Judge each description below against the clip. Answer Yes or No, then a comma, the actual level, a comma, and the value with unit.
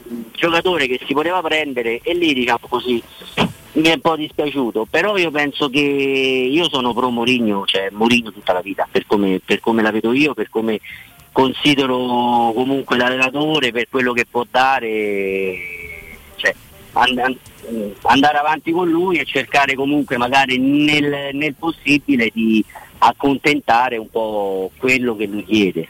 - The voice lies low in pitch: Yes, low, 125 Hz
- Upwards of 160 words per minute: No, average, 155 wpm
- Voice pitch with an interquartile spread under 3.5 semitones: No, average, 4.8 semitones